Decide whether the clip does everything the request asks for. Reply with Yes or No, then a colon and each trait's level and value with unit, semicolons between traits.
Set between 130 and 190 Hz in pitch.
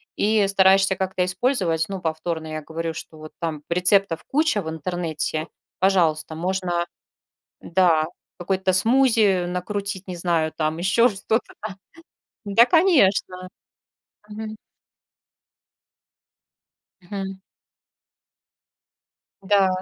Yes: medium, 185 Hz